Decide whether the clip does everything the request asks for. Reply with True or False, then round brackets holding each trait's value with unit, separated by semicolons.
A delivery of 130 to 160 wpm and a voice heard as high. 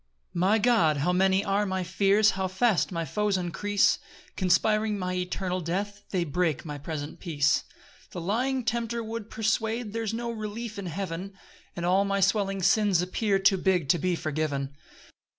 False (170 wpm; 195 Hz)